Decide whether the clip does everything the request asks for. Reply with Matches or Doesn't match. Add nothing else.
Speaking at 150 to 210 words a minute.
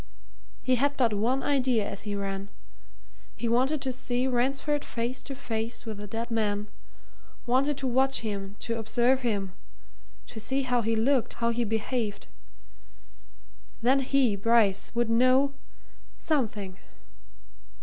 Doesn't match